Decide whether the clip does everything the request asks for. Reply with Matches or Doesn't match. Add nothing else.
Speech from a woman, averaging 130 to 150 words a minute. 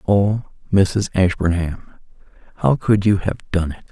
Doesn't match